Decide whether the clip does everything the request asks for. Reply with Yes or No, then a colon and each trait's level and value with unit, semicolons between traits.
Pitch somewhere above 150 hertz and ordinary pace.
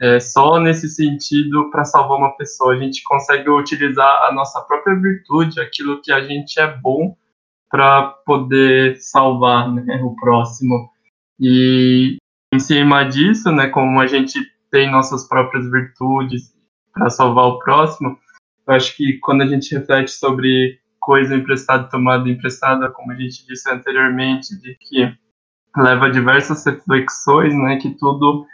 No: low, 135 Hz; average, 145 wpm